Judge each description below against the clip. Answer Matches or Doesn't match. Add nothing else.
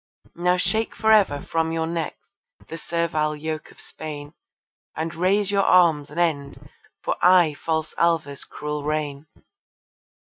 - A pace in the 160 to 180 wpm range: Doesn't match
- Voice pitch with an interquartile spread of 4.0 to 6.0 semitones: Doesn't match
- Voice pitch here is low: Doesn't match